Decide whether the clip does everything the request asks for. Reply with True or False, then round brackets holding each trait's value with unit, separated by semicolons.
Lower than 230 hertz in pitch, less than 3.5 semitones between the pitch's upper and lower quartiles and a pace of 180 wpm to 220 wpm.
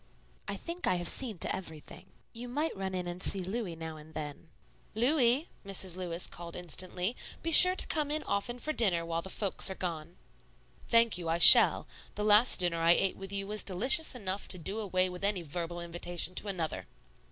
False (185 Hz; 4.5 semitones; 200 wpm)